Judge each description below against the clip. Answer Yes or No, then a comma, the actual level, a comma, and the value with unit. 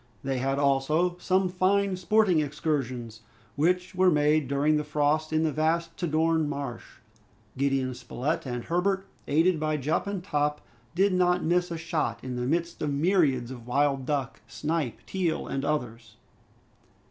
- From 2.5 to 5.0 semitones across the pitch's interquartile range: Yes, average, 4.2 semitones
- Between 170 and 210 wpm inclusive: No, average, 155 wpm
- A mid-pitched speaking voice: Yes, medium, 150 Hz